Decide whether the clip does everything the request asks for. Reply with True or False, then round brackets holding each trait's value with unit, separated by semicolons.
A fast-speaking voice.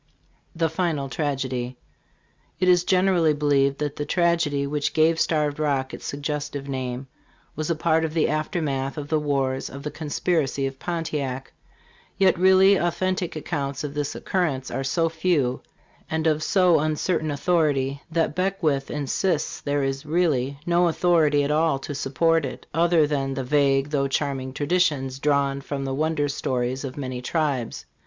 False (160 wpm)